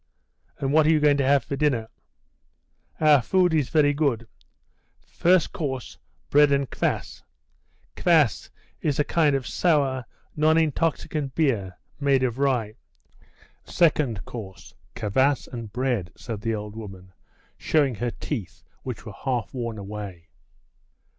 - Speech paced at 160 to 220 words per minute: No, slow, 135 wpm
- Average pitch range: Yes, average, 5.0 semitones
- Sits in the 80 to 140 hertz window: Yes, low, 135 Hz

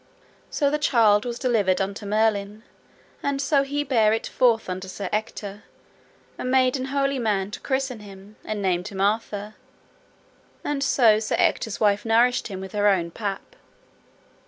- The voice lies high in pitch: Yes, high, 215 Hz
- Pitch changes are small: No, average, 4.2 semitones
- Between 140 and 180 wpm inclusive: Yes, average, 160 wpm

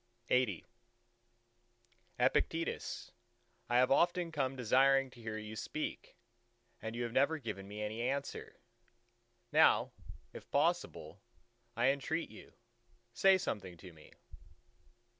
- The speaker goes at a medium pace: No, slow, 115 wpm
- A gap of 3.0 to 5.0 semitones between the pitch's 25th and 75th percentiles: Yes, average, 4.4 semitones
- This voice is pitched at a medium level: No, low, 125 Hz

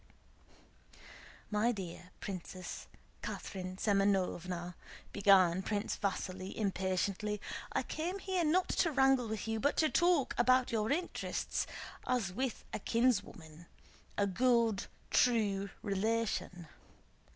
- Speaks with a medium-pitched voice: No, high, 210 Hz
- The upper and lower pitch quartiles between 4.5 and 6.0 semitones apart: Yes, average, 5.0 semitones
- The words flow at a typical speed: No, slow, 110 wpm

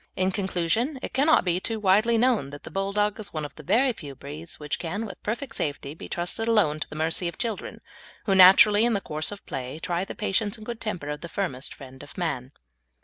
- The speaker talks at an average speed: No, fast, 230 wpm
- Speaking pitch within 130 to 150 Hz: No, medium, 185 Hz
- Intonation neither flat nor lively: No, wide, 5.9 semitones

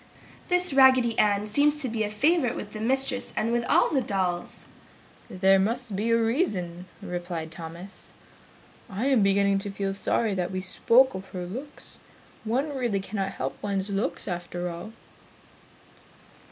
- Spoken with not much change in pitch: No, average, 4.8 semitones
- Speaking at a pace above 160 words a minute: No, average, 155 wpm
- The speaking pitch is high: Yes, high, 210 Hz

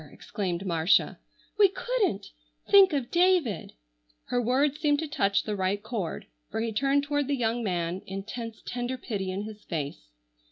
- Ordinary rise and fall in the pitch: No, wide, 6.6 semitones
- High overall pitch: Yes, high, 230 Hz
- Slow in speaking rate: No, average, 160 wpm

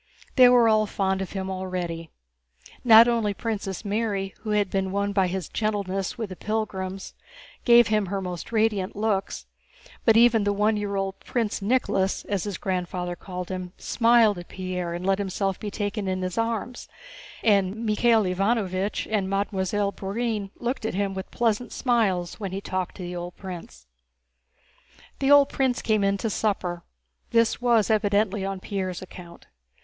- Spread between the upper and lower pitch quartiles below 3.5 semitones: Yes, average, 2.8 semitones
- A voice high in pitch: Yes, high, 200 Hz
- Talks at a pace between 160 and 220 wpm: Yes, average, 165 wpm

